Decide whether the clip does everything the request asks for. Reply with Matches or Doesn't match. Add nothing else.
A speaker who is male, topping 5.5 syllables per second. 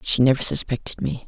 Doesn't match